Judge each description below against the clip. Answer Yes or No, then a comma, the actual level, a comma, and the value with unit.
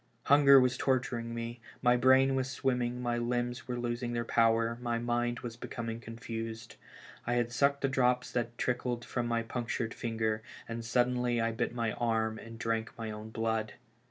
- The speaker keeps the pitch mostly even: Yes, narrow, 1.3 semitones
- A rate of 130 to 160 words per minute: No, average, 175 wpm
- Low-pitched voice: Yes, low, 120 Hz